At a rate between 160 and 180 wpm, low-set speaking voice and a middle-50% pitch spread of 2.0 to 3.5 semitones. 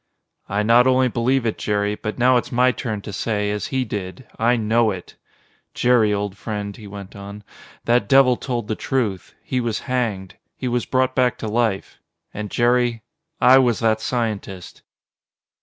Yes: average, 175 wpm; low, 115 Hz; average, 3.2 semitones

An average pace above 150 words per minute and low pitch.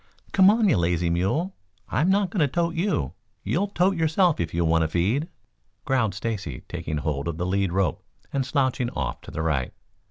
Yes: average, 195 wpm; low, 115 Hz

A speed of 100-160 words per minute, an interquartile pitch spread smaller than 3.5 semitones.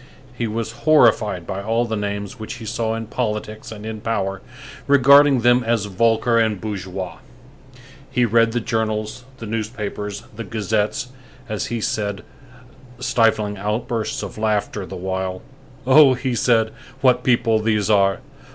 Yes: average, 145 wpm; narrow, 2.4 semitones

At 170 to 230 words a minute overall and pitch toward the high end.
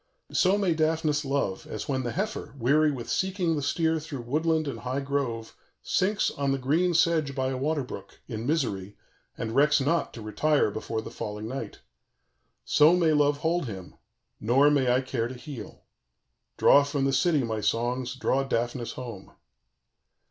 No: average, 175 wpm; medium, 140 Hz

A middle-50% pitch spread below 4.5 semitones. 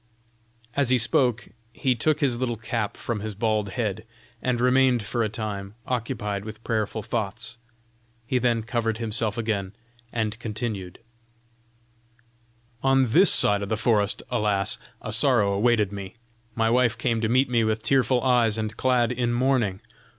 Yes: narrow, 2.6 semitones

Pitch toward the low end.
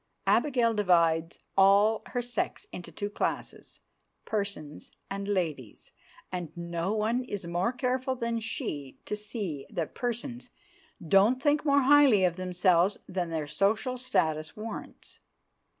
No: high, 200 Hz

